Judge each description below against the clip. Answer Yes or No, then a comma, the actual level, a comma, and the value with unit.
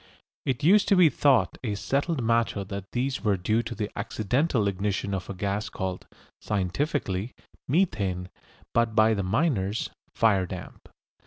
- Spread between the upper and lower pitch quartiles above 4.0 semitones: Yes, average, 4.9 semitones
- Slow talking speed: No, average, 150 wpm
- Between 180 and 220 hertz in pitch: No, low, 110 Hz